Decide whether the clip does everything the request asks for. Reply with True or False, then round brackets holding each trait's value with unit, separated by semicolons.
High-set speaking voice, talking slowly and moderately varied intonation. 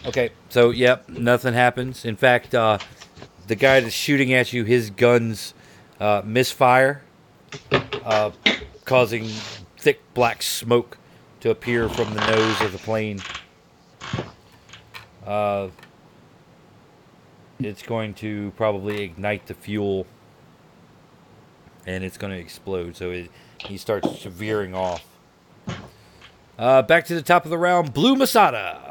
False (110 Hz; 125 wpm; 3.7 semitones)